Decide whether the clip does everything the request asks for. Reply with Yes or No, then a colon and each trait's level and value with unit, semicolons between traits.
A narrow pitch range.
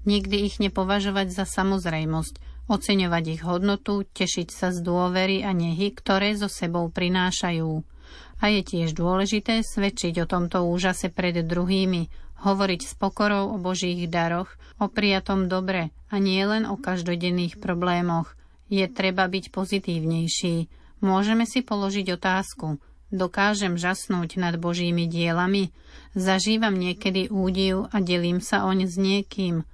Yes: narrow, 2.2 semitones